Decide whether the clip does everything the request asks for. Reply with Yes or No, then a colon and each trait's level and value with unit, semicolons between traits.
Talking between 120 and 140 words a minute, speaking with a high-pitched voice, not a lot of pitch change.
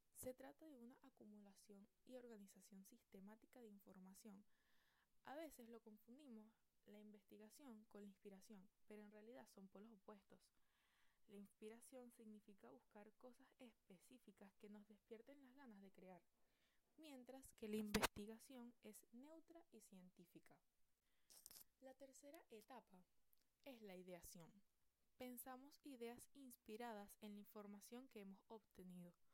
No: slow, 125 wpm; high, 220 Hz; average, 3.7 semitones